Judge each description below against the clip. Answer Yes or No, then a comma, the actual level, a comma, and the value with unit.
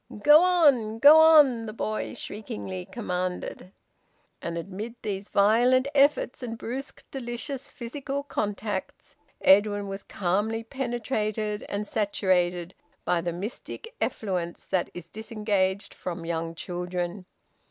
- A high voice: Yes, high, 210 Hz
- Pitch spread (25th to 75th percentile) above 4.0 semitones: Yes, average, 4.8 semitones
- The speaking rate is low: Yes, slow, 115 wpm